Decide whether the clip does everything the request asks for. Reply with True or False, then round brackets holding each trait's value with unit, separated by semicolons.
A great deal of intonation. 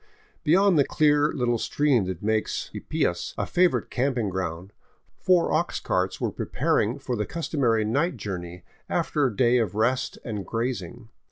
True (5.9 semitones)